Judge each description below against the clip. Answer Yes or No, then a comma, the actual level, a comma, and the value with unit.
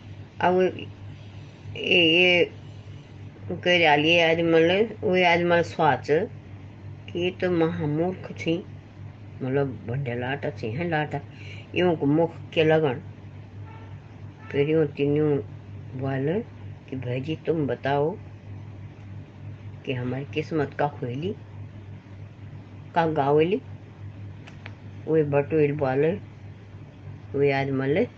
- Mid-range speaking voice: No, low, 125 Hz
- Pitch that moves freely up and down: Yes, wide, 6.2 semitones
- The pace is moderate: No, slow, 85 wpm